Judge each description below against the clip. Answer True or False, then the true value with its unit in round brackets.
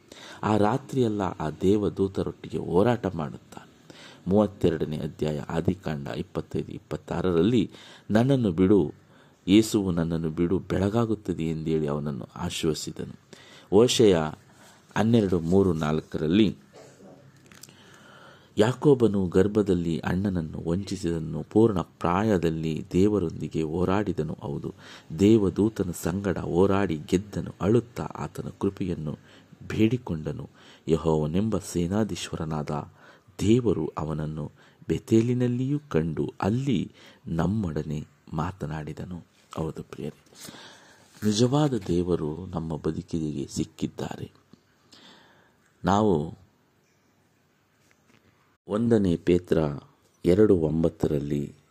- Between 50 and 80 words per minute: True (70 wpm)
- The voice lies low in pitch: True (90 Hz)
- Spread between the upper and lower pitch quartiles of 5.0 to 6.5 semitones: False (4.6 semitones)